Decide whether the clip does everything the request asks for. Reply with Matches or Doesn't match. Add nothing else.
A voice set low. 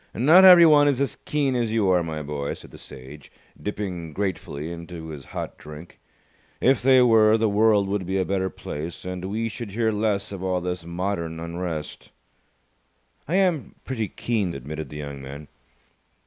Matches